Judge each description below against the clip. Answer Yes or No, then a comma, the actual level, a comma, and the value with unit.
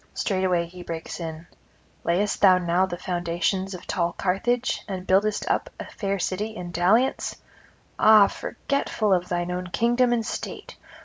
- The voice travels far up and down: No, average, 3.1 semitones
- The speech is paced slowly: No, average, 160 wpm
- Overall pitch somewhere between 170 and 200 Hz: Yes, medium, 185 Hz